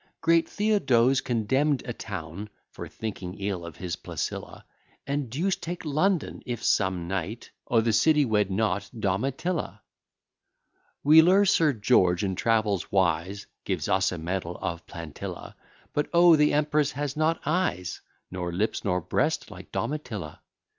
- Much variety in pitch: Yes, wide, 8.0 semitones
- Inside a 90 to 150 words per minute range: Yes, average, 140 wpm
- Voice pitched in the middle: No, low, 115 Hz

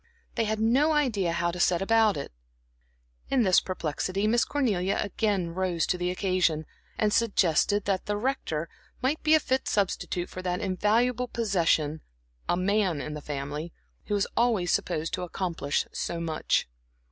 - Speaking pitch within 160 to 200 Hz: Yes, high, 190 Hz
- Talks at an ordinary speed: Yes, average, 160 wpm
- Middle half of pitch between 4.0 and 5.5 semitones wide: Yes, average, 4.5 semitones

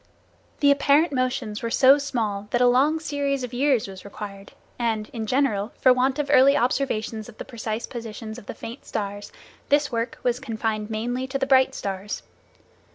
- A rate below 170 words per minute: No, average, 180 wpm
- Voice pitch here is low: No, high, 245 Hz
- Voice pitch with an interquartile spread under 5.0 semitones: Yes, average, 3.9 semitones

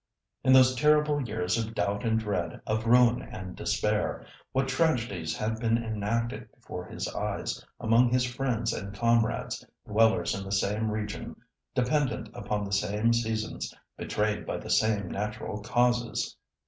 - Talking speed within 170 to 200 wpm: No, average, 145 wpm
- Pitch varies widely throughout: No, average, 2.7 semitones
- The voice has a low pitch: Yes, low, 110 Hz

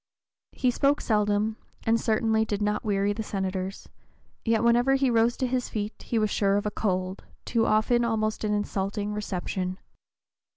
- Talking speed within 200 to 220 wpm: No, average, 165 wpm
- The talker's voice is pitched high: Yes, high, 215 Hz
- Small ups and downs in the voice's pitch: Yes, narrow, 2.1 semitones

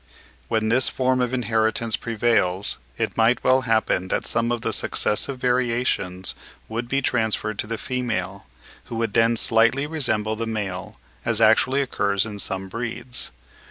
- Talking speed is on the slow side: No, average, 155 wpm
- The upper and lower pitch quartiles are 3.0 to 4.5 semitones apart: No, narrow, 2.4 semitones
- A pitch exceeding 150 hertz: No, low, 115 Hz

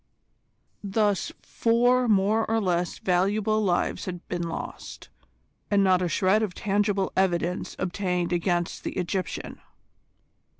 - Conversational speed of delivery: No, slow, 120 wpm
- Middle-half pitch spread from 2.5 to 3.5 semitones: Yes, average, 2.8 semitones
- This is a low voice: No, high, 190 Hz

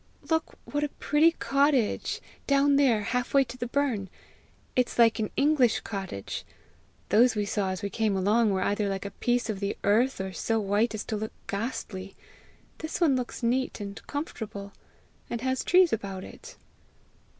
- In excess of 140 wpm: Yes, average, 170 wpm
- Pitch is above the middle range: Yes, high, 225 Hz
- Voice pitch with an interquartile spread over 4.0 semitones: Yes, average, 4.7 semitones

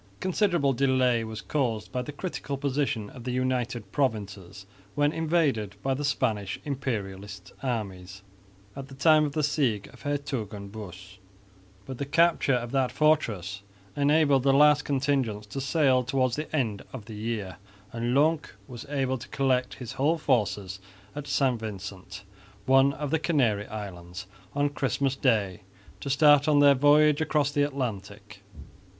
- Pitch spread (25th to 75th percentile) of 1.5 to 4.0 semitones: No, average, 5.1 semitones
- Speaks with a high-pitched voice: No, low, 130 Hz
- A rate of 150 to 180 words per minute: Yes, average, 155 wpm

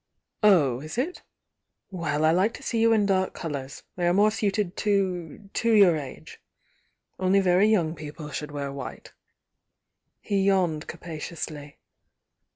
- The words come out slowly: No, average, 150 wpm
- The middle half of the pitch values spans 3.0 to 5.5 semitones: Yes, average, 4.8 semitones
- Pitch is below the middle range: No, medium, 180 Hz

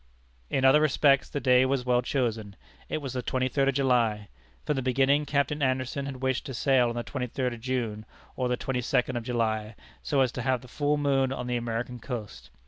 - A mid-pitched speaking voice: No, low, 130 Hz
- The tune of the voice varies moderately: No, narrow, 2.1 semitones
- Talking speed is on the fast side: Yes, fast, 220 wpm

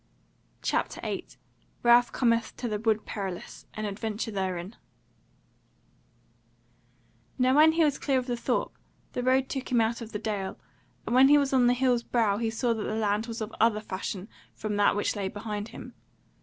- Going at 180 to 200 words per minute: Yes, average, 185 wpm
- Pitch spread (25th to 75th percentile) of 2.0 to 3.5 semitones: Yes, average, 3.0 semitones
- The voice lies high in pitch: Yes, high, 225 Hz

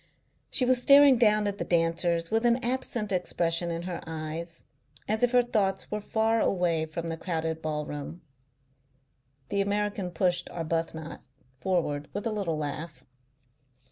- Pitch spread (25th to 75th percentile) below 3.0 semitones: No, average, 4.4 semitones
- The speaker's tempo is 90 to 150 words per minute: Yes, average, 145 wpm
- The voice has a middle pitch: Yes, medium, 175 Hz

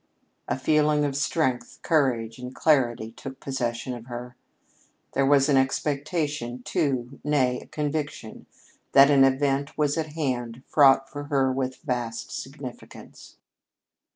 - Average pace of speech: No, slow, 130 wpm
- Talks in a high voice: No, low, 135 Hz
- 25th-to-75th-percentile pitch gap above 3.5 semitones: No, average, 2.7 semitones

